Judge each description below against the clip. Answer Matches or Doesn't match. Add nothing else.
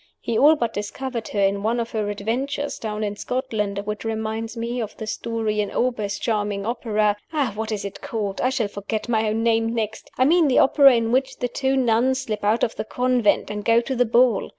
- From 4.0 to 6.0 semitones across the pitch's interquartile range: Doesn't match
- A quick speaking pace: Matches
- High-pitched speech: Matches